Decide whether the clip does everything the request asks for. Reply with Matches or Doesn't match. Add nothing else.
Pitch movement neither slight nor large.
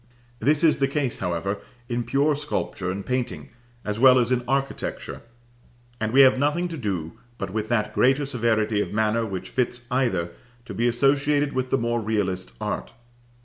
Matches